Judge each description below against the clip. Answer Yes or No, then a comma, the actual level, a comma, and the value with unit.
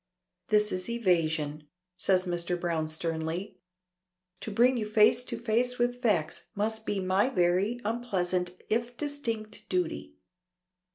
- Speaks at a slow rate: Yes, slow, 125 wpm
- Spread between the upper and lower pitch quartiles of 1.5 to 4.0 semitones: No, average, 4.9 semitones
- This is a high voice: Yes, high, 200 Hz